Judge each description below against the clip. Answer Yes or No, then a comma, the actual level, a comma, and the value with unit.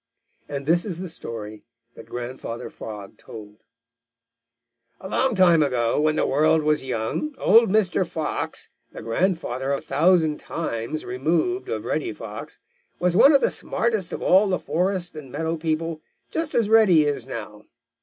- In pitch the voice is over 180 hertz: No, medium, 160 Hz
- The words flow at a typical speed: Yes, average, 155 wpm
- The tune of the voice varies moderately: No, wide, 6.3 semitones